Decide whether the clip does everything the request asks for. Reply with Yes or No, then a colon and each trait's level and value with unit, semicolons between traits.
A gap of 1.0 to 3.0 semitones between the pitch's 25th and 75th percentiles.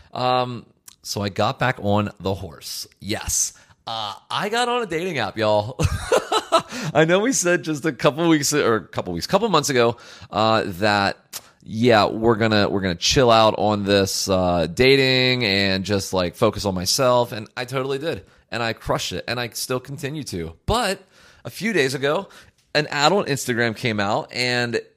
No: wide, 5.5 semitones